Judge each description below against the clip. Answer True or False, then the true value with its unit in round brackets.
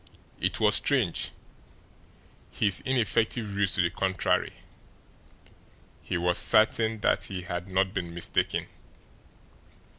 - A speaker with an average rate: False (110 wpm)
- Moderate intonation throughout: True (3.6 semitones)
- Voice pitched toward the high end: False (95 Hz)